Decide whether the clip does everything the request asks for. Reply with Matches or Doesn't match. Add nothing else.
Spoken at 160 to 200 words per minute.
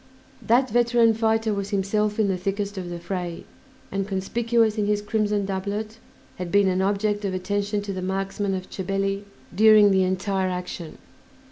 Matches